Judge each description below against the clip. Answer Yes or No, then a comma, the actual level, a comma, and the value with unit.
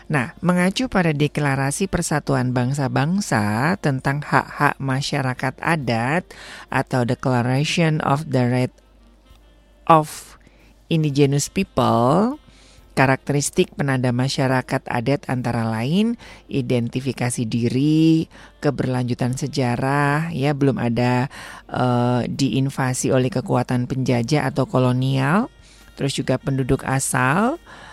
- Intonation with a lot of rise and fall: No, average, 2.9 semitones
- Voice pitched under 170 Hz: Yes, low, 135 Hz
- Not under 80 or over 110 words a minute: Yes, average, 90 wpm